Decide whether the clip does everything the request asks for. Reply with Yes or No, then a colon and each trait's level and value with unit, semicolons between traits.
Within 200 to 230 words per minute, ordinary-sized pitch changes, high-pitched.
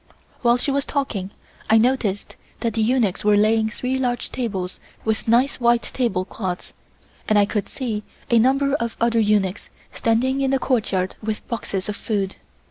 No: average, 170 wpm; average, 3.4 semitones; high, 225 Hz